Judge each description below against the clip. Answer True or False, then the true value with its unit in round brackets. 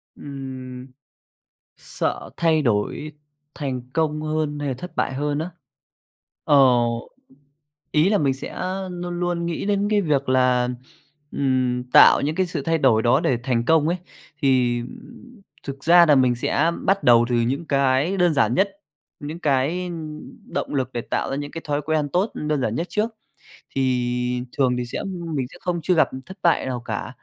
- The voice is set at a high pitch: False (145 Hz)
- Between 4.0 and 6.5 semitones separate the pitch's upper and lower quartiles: True (4.7 semitones)